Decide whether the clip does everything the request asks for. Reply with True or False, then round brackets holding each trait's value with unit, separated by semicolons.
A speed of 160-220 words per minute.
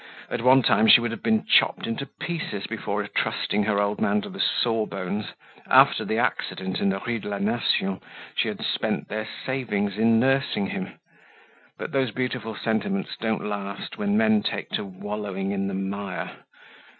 True (175 wpm)